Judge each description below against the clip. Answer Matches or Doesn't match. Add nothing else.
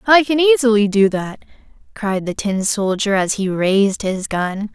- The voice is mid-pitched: Doesn't match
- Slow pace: Doesn't match